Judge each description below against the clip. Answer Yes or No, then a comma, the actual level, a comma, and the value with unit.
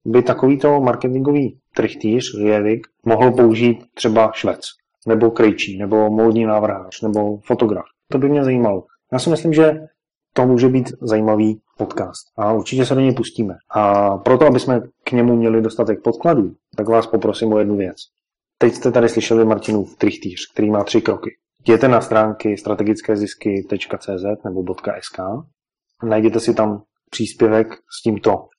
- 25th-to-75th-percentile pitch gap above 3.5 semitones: No, average, 2.8 semitones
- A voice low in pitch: Yes, low, 115 Hz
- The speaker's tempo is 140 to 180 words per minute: Yes, average, 155 wpm